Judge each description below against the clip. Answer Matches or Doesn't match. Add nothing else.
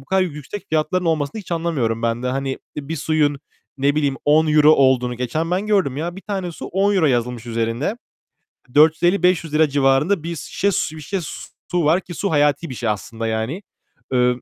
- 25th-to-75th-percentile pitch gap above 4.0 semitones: Matches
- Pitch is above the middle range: Doesn't match